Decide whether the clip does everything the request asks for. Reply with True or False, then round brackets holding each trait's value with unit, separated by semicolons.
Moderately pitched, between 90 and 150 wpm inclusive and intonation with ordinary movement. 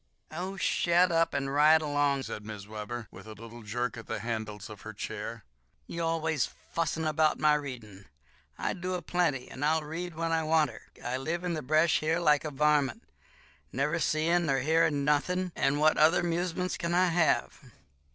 False (155 Hz; 185 wpm; 4.3 semitones)